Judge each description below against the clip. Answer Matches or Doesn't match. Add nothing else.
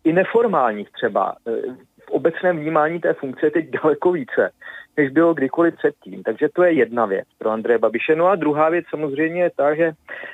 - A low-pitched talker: Doesn't match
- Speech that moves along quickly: Matches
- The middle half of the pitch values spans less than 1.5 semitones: Doesn't match